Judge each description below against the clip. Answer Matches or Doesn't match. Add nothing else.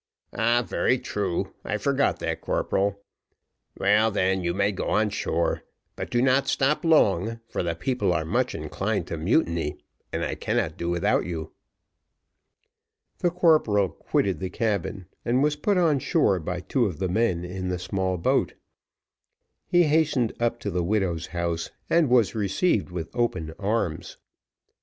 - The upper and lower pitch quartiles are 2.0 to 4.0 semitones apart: Doesn't match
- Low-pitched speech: Matches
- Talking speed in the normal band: Matches